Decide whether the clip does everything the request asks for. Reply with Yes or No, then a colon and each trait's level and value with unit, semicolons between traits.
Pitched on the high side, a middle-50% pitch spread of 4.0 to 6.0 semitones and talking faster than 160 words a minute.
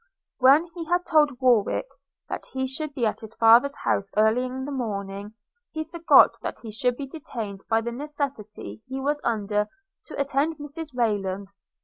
Yes: very high, 255 Hz; average, 5.0 semitones; average, 170 wpm